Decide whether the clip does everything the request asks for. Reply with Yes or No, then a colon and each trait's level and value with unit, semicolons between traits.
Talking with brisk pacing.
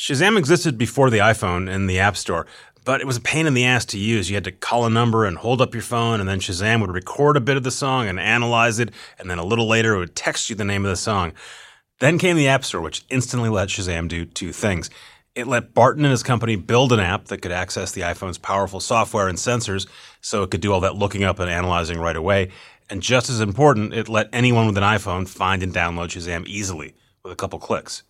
Yes: fast, 250 wpm